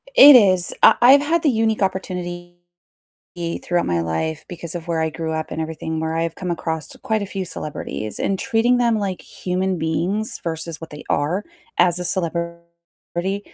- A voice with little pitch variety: No, average, 3.5 semitones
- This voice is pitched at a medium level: Yes, medium, 175 Hz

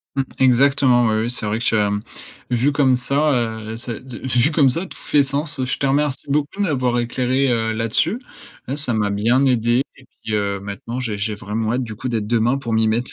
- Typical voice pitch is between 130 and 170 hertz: No, low, 120 Hz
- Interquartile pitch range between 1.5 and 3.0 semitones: No, average, 3.5 semitones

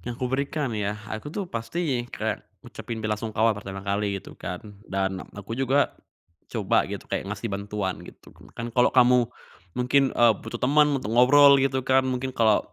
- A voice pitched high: No, low, 120 Hz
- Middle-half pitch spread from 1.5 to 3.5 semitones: No, average, 4.1 semitones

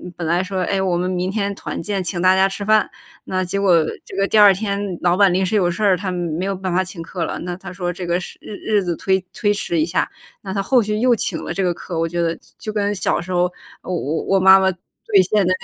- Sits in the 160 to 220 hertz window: Yes, high, 190 Hz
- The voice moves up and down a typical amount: No, narrow, 2.1 semitones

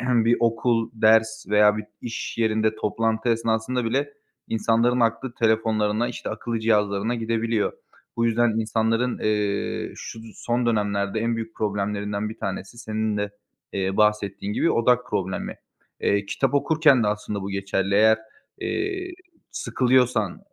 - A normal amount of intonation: No, narrow, 2.0 semitones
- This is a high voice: No, low, 110 Hz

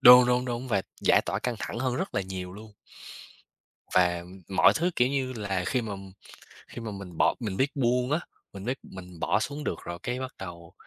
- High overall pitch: No, low, 115 Hz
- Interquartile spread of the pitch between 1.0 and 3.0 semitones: No, average, 5.1 semitones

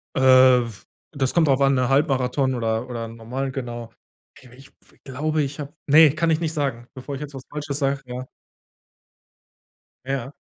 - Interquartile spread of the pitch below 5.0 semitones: Yes, narrow, 2.5 semitones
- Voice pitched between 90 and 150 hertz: Yes, low, 135 Hz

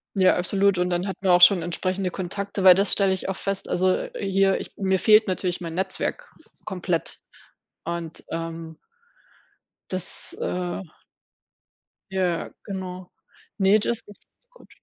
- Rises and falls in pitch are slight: Yes, narrow, 1.8 semitones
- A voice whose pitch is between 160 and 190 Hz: Yes, medium, 185 Hz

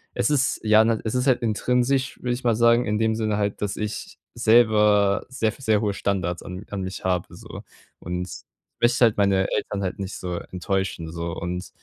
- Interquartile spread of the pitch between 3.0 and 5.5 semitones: Yes, average, 3.7 semitones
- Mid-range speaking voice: No, low, 105 Hz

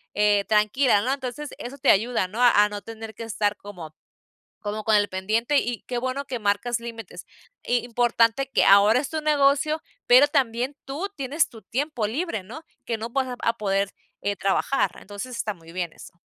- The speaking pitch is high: Yes, high, 230 Hz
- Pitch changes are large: No, average, 4.4 semitones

